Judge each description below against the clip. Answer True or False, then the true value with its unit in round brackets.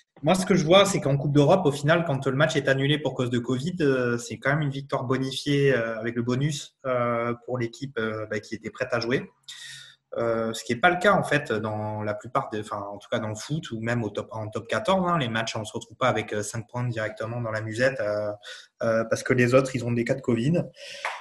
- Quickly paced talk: True (240 wpm)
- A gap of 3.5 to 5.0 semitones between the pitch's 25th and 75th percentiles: True (3.8 semitones)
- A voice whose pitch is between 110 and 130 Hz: True (125 Hz)